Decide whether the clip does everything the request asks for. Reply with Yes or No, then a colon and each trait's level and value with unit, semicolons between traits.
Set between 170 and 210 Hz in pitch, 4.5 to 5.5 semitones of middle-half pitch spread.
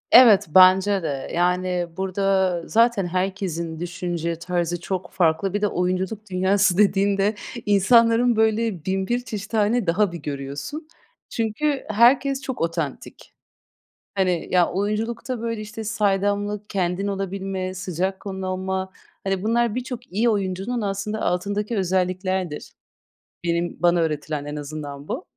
No: high, 190 Hz; average, 3.1 semitones